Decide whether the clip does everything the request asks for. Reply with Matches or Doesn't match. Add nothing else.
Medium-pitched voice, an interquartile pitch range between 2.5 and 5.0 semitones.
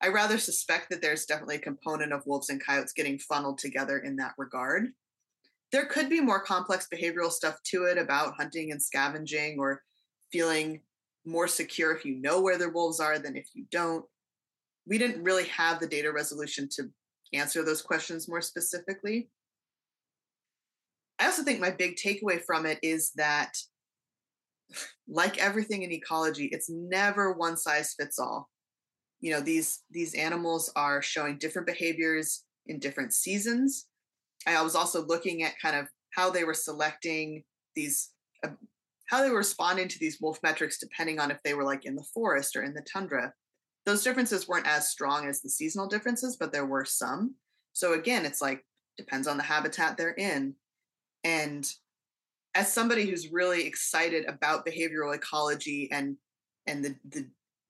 Matches